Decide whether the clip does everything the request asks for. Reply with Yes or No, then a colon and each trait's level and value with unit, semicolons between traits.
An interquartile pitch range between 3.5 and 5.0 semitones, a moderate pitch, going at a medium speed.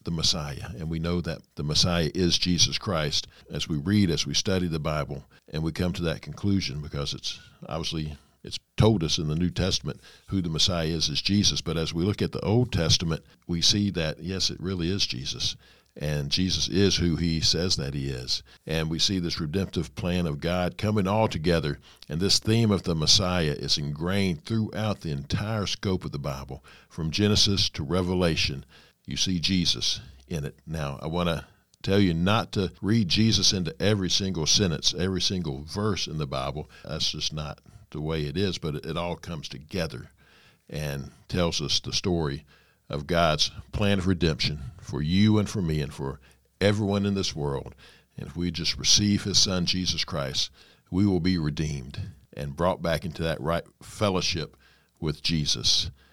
No: average, 4.1 semitones; very low, 85 Hz; average, 190 wpm